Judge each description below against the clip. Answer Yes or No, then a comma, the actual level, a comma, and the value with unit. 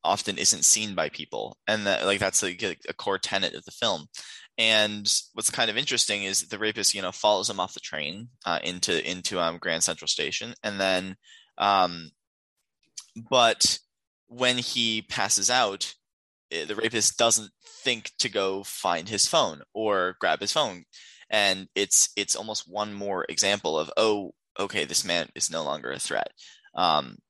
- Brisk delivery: No, average, 170 wpm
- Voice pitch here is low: Yes, low, 105 Hz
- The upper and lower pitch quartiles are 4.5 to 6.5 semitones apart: No, average, 2.8 semitones